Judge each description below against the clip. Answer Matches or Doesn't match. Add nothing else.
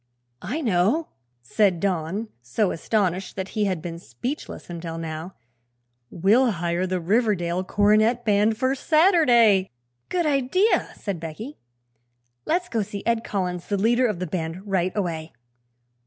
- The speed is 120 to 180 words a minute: Matches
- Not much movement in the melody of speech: Doesn't match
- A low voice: Doesn't match